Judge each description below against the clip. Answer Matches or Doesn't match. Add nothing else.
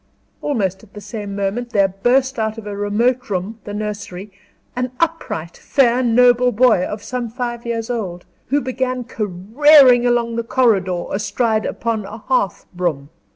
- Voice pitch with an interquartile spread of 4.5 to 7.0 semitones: Doesn't match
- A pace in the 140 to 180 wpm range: Matches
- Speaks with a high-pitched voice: Matches